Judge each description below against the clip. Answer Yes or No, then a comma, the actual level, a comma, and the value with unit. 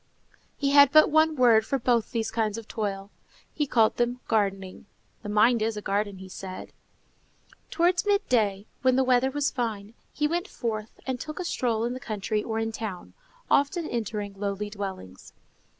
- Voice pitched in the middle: No, high, 225 Hz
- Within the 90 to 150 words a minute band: No, average, 175 wpm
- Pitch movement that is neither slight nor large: Yes, average, 4.2 semitones